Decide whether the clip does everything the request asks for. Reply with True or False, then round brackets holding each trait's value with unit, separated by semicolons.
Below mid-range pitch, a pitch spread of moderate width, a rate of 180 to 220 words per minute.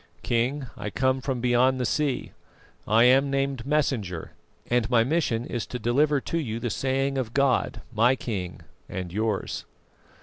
False (125 Hz; 3.2 semitones; 160 wpm)